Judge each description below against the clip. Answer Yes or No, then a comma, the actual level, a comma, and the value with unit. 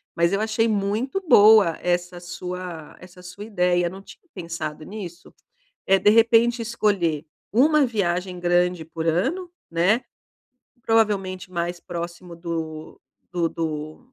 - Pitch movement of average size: Yes, average, 3.9 semitones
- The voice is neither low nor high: Yes, medium, 180 Hz